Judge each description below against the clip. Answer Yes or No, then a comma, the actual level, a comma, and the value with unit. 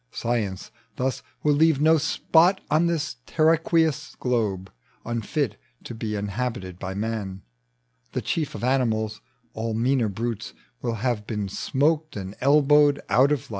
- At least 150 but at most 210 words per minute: No, average, 140 wpm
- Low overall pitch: Yes, low, 125 Hz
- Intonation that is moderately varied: No, wide, 5.7 semitones